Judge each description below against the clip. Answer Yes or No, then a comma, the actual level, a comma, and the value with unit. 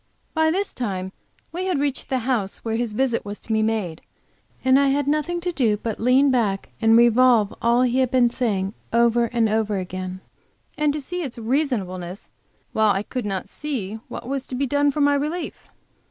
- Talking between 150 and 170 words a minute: No, average, 195 wpm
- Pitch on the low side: No, high, 240 Hz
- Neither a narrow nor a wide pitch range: Yes, average, 4.7 semitones